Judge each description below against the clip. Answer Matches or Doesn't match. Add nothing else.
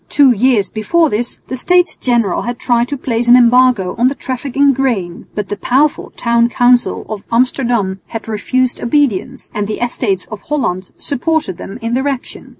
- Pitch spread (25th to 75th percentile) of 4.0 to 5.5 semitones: Doesn't match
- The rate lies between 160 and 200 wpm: Matches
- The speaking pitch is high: Matches